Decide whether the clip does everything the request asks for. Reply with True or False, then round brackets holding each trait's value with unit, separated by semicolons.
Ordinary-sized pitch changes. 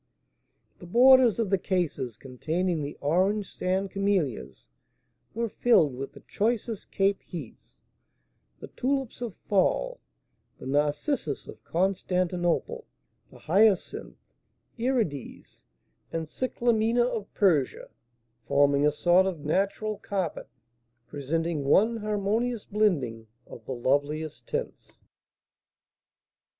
False (6.7 semitones)